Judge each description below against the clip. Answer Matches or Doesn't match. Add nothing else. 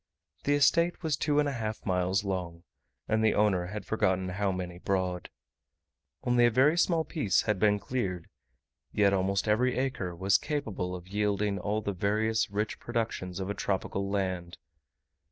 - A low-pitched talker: Matches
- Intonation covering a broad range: Doesn't match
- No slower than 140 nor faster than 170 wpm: Matches